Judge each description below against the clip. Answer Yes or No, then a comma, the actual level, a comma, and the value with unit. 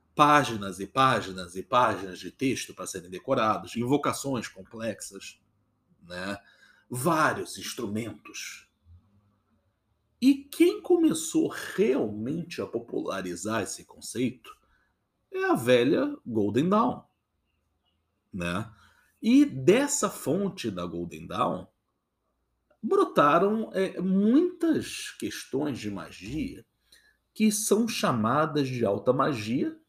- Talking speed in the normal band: No, slow, 95 wpm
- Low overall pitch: Yes, low, 130 Hz